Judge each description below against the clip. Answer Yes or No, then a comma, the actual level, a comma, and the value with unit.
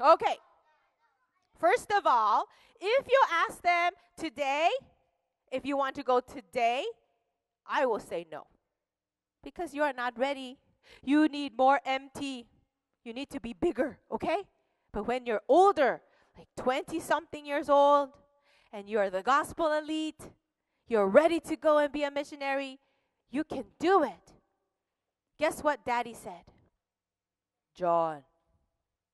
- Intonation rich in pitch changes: No, average, 4.8 semitones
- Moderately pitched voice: No, very high, 275 Hz